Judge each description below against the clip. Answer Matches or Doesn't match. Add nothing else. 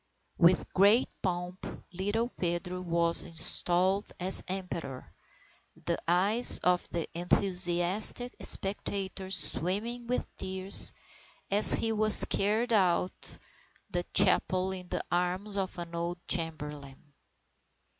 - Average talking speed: Doesn't match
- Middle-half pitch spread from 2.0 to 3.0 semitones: Matches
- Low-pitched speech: Doesn't match